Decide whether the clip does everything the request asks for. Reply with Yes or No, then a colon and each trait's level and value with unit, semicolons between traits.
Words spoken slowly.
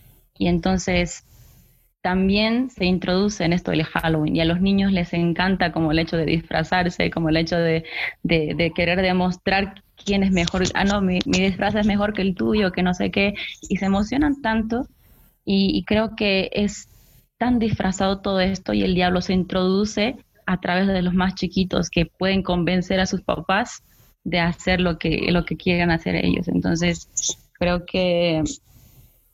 No: average, 180 wpm